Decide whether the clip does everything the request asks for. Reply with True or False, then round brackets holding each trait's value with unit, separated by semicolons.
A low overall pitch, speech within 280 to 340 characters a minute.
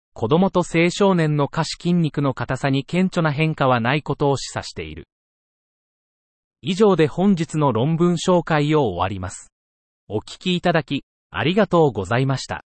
False (145 Hz; 310 characters per minute)